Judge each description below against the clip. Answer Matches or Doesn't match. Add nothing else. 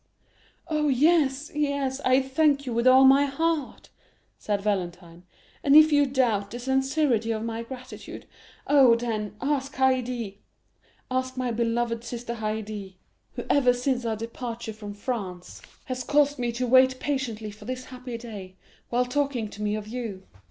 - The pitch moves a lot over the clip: Doesn't match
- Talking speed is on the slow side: Doesn't match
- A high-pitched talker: Matches